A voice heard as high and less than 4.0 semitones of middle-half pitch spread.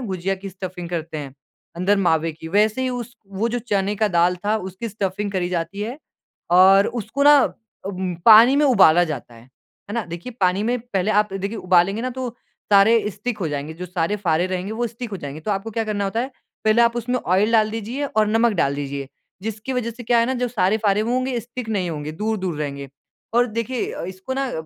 No: high, 205 Hz; average, 4.4 semitones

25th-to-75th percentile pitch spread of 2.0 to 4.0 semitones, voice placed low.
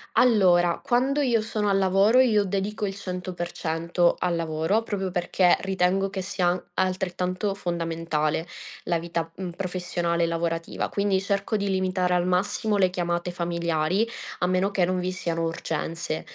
No: narrow, 2.4 semitones; medium, 185 Hz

